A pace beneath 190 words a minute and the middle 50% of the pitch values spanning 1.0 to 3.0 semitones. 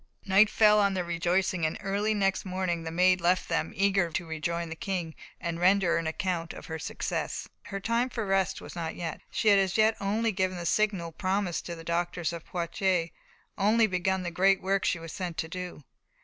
No: fast, 205 wpm; average, 2.7 semitones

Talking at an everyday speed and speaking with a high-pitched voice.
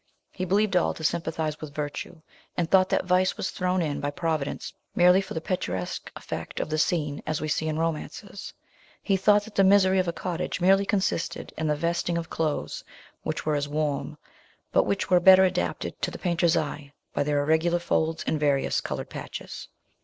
No: average, 195 wpm; medium, 165 Hz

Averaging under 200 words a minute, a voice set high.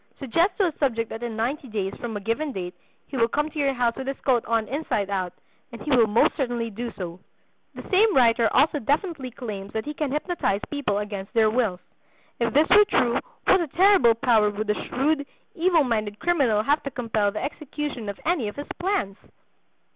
No: fast, 205 wpm; high, 245 Hz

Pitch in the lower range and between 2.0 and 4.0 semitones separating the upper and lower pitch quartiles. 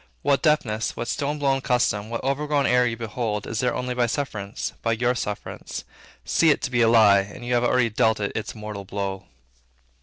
Yes: low, 120 Hz; average, 3.0 semitones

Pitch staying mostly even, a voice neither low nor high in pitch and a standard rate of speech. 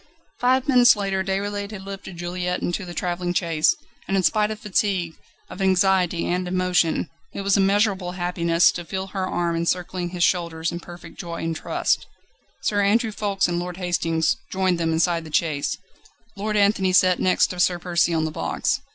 Yes: narrow, 2.2 semitones; medium, 180 Hz; average, 180 wpm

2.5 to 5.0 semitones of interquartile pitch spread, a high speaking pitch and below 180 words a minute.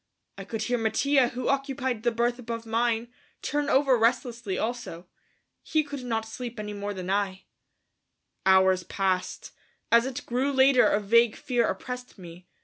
Yes: average, 3.5 semitones; high, 235 Hz; average, 155 wpm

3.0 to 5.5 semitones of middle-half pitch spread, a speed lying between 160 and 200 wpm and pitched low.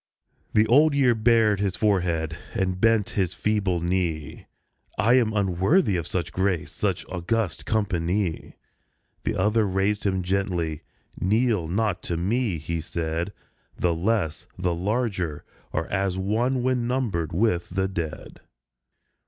No: average, 4.1 semitones; slow, 135 wpm; very low, 95 Hz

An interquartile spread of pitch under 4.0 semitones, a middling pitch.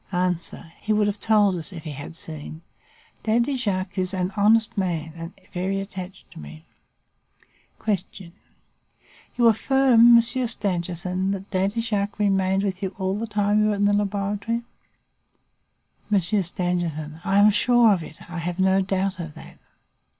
No: average, 2.9 semitones; high, 195 Hz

